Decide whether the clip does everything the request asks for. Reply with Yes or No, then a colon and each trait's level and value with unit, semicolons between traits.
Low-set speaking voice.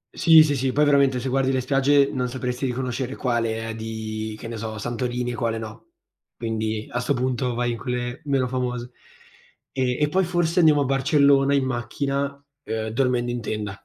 Yes: low, 125 Hz